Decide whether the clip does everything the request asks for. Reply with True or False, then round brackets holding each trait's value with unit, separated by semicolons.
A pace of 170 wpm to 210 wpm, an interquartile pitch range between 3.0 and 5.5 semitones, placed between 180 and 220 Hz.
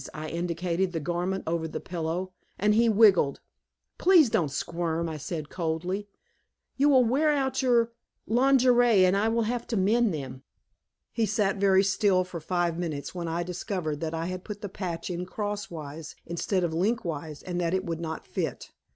True (175 wpm; 4.3 semitones; 185 Hz)